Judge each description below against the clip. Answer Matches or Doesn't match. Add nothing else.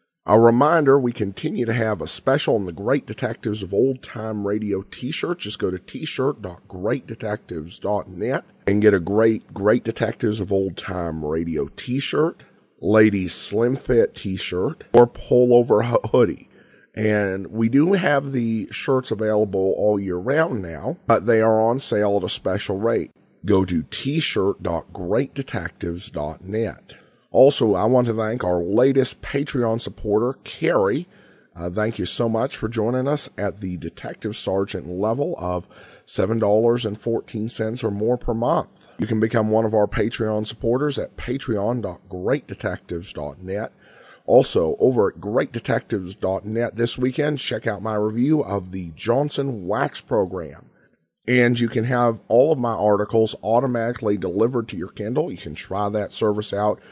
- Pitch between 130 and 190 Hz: Doesn't match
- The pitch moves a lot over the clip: Doesn't match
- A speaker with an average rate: Matches